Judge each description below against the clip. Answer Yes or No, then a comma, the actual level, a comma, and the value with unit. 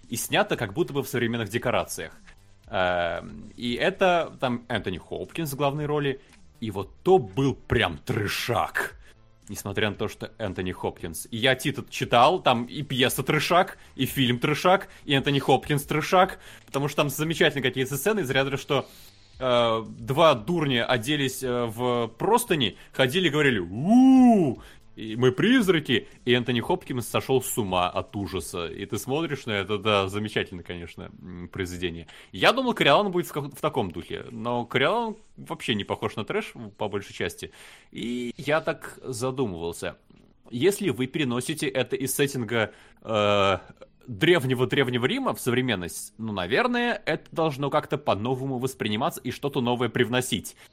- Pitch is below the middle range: Yes, low, 130 Hz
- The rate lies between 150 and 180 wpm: Yes, average, 155 wpm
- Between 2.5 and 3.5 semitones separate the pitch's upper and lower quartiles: No, average, 5.2 semitones